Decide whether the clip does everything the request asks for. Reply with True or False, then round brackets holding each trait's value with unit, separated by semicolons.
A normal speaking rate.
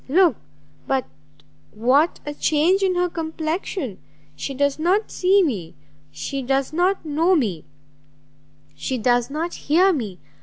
False (130 wpm)